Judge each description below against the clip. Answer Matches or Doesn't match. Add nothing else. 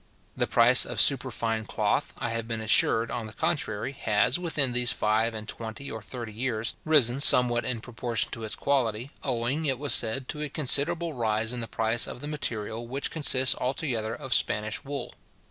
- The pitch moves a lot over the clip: Doesn't match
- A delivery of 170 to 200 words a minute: Matches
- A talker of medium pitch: Doesn't match